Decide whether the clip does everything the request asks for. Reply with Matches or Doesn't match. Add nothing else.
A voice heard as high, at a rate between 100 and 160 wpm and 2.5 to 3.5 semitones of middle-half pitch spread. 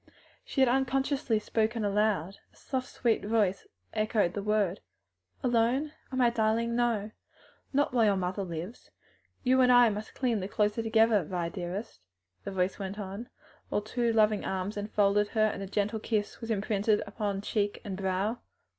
Doesn't match